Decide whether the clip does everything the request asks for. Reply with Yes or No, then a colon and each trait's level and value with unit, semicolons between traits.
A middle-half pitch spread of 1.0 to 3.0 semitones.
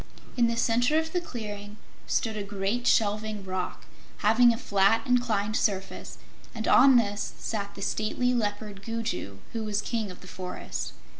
Yes: narrow, 2.6 semitones